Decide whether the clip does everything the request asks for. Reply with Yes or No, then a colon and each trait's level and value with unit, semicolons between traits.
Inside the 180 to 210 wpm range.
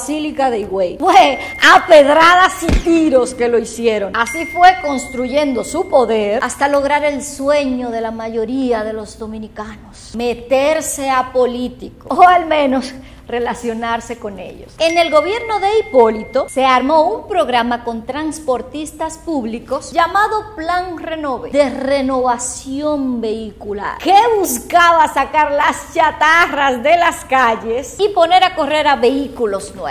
No: average, 135 wpm